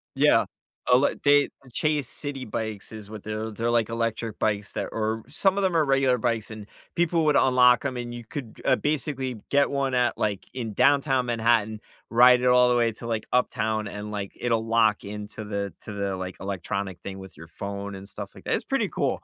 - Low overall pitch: Yes, low, 115 Hz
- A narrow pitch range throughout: No, average, 3.5 semitones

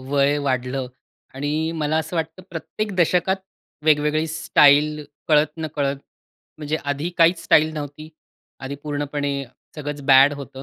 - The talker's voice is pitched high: No, medium, 150 Hz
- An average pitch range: No, narrow, 1.9 semitones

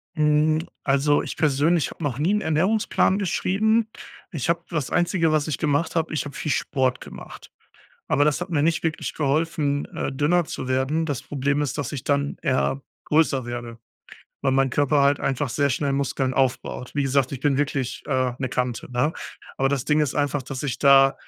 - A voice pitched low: No, medium, 145 Hz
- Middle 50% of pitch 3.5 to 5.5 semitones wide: No, narrow, 2.6 semitones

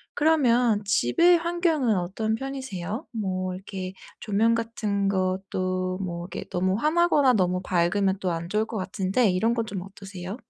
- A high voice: Yes, high, 200 Hz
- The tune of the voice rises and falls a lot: No, average, 4.2 semitones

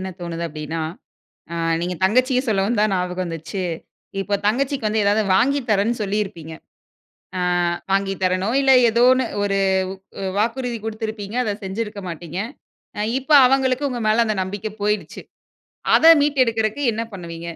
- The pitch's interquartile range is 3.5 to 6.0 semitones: Yes, average, 4.1 semitones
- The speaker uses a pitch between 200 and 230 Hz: Yes, high, 210 Hz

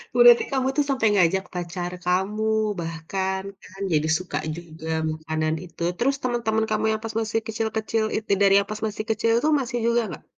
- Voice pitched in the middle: No, high, 210 Hz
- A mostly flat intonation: No, average, 4.3 semitones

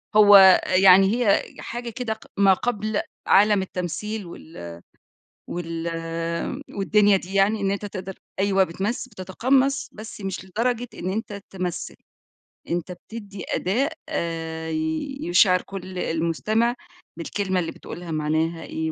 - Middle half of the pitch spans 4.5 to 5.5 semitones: No, average, 3.4 semitones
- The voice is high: Yes, high, 195 Hz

